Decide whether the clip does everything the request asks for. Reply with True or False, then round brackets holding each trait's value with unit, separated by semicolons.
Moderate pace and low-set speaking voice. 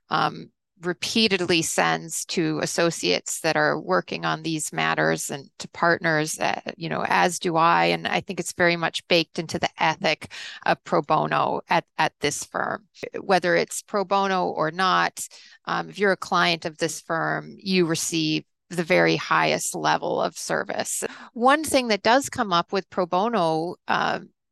False (170 wpm; 170 Hz)